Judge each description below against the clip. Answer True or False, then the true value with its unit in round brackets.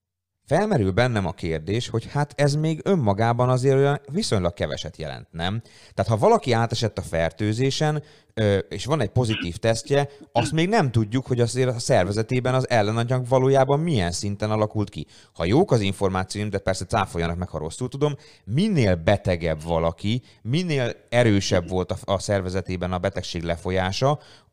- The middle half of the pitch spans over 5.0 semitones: True (5.6 semitones)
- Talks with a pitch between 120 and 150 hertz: False (110 Hz)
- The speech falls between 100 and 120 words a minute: False (155 wpm)